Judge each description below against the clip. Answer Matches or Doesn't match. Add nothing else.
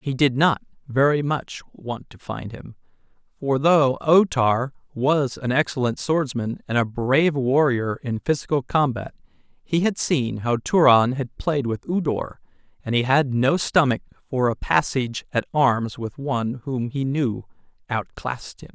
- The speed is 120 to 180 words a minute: Matches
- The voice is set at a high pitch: Doesn't match